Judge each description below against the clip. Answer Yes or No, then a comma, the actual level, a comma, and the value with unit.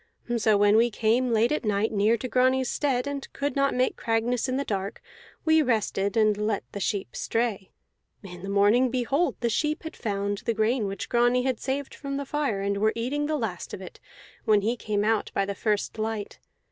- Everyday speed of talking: No, fast, 210 wpm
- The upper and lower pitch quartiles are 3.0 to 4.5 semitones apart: Yes, average, 3.9 semitones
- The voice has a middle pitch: No, high, 225 Hz